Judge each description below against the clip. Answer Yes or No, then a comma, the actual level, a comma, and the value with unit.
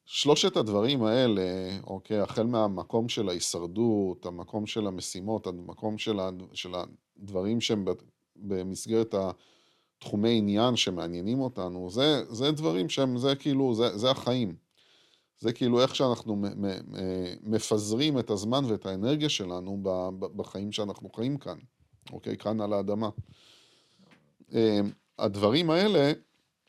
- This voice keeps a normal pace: Yes, average, 110 wpm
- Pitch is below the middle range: Yes, low, 110 Hz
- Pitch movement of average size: Yes, average, 4.2 semitones